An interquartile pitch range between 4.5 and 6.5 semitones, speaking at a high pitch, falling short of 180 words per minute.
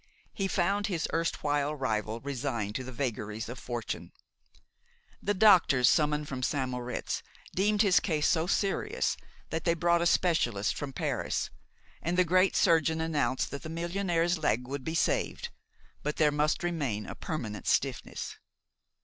No: average, 5.1 semitones; medium, 155 Hz; average, 150 wpm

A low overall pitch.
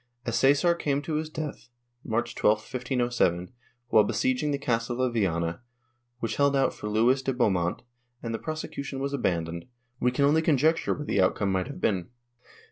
Yes: low, 125 Hz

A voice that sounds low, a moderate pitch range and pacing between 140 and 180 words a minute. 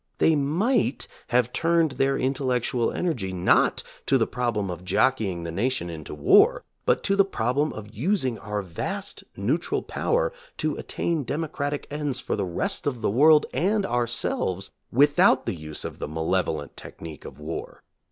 No: low, 125 Hz; wide, 7.9 semitones; average, 160 wpm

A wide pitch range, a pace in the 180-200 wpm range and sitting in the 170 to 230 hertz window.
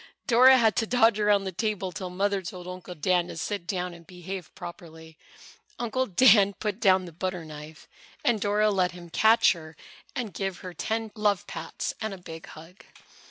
No: average, 3.4 semitones; average, 185 wpm; high, 190 Hz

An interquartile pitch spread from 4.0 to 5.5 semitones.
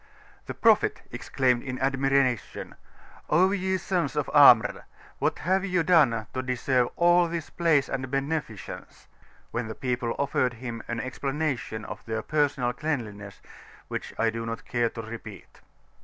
Yes: average, 4.6 semitones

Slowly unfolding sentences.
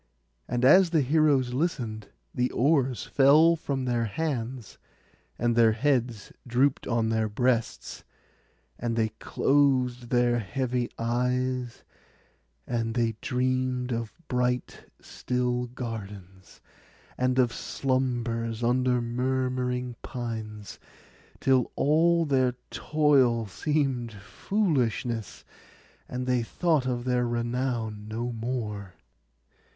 Yes: slow, 105 wpm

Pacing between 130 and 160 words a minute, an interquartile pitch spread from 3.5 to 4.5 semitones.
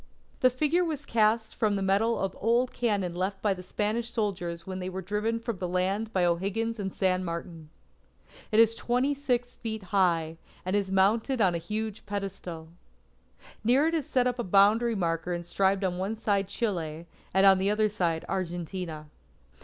No: average, 175 wpm; average, 3.9 semitones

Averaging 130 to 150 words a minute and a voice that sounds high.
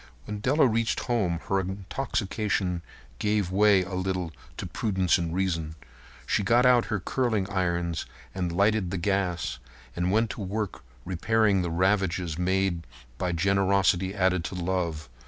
No: average, 145 wpm; very low, 95 Hz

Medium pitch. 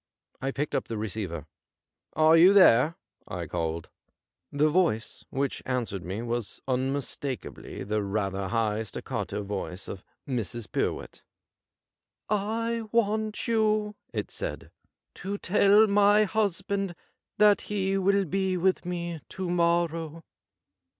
Yes: medium, 165 Hz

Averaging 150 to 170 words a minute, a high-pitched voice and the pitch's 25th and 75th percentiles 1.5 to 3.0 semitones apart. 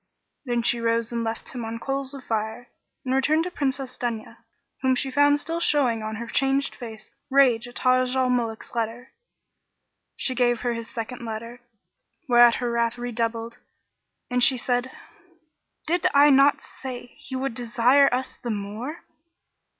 Yes: average, 165 wpm; high, 245 Hz; narrow, 2.5 semitones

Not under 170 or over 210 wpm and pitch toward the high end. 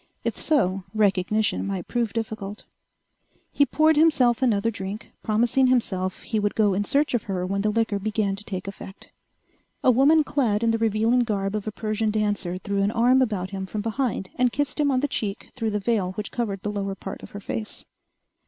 Yes: average, 200 wpm; high, 215 Hz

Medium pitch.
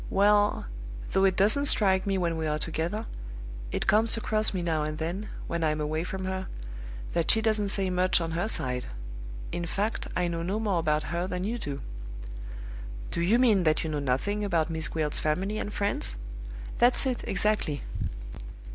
Yes: medium, 180 Hz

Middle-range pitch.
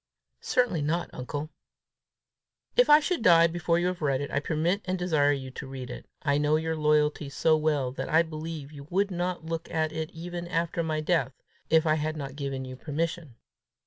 Yes: medium, 155 Hz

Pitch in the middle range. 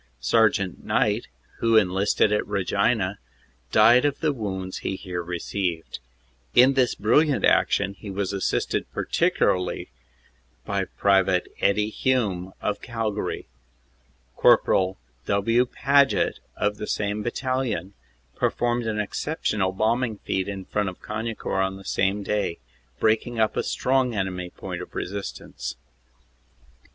No: low, 105 Hz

